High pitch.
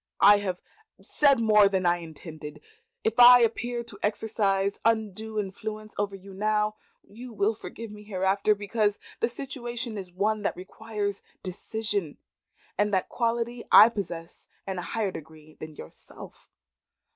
Yes: high, 210 Hz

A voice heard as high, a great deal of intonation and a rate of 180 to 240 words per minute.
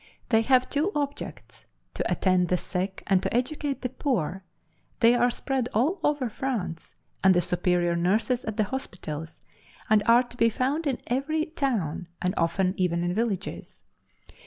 No: high, 225 Hz; wide, 6.6 semitones; average, 160 wpm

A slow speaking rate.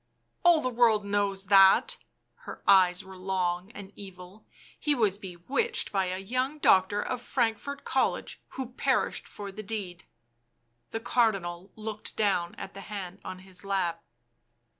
No: average, 165 wpm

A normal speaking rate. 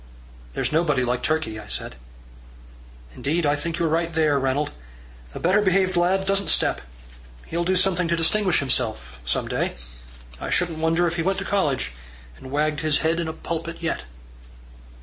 Yes: average, 170 wpm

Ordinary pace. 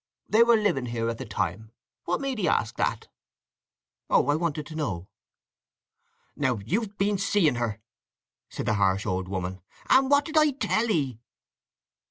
Yes: average, 160 wpm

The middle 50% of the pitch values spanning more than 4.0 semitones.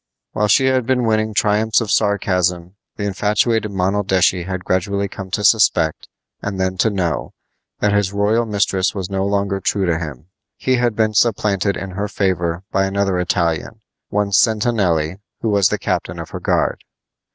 No: narrow, 2.4 semitones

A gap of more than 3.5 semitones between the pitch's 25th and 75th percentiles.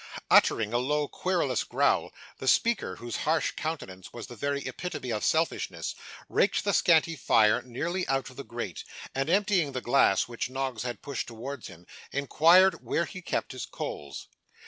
Yes: average, 5.2 semitones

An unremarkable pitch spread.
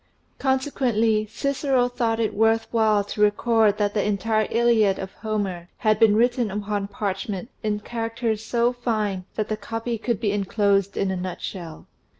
No: narrow, 2.3 semitones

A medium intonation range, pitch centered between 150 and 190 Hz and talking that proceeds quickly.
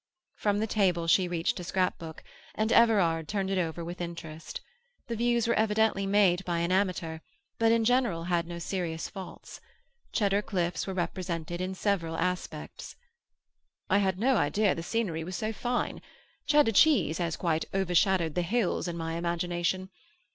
No: average, 3.5 semitones; medium, 185 Hz; average, 160 wpm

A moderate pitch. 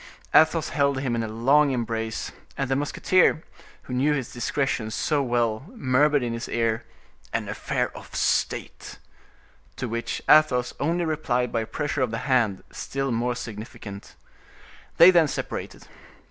No: low, 125 Hz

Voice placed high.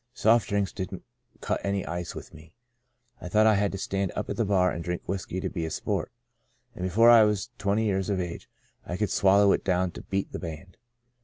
No: very low, 95 Hz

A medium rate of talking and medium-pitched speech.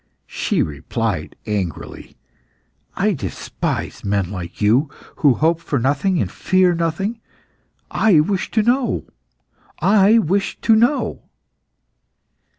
No: slow, 110 wpm; medium, 165 Hz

